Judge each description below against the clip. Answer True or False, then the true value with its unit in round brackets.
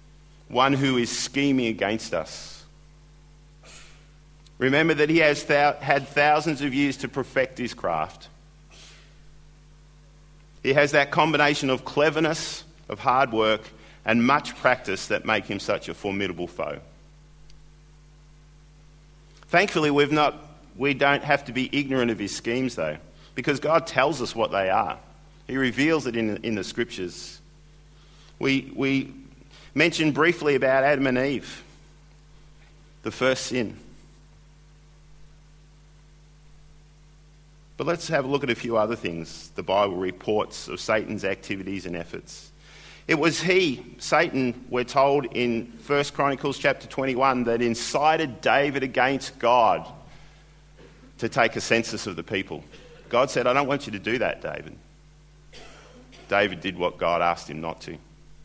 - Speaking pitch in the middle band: True (145 Hz)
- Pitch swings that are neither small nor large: True (3.5 semitones)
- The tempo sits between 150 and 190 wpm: False (140 wpm)